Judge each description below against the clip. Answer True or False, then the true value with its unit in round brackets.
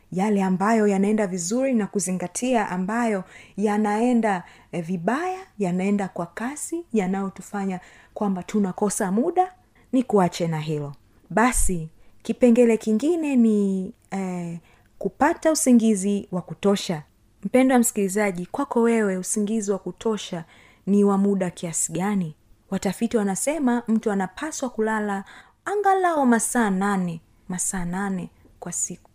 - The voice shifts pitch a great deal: False (3.9 semitones)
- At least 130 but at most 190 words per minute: False (110 wpm)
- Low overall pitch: False (200 Hz)